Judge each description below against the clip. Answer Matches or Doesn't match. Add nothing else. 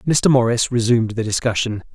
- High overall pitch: Doesn't match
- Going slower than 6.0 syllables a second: Matches